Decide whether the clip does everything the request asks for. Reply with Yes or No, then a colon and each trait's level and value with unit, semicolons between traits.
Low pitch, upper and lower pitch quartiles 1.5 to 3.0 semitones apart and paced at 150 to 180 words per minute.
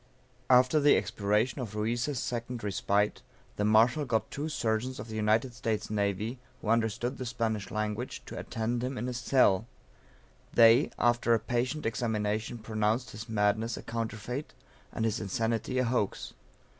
Yes: low, 115 Hz; narrow, 2.4 semitones; average, 155 wpm